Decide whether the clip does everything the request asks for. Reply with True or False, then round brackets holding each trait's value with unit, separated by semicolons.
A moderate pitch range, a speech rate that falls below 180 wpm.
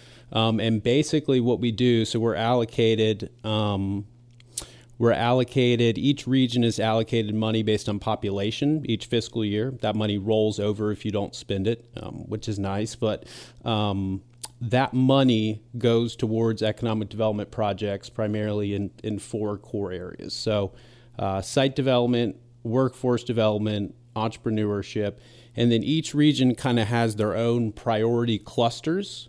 False (2.1 semitones; 140 wpm)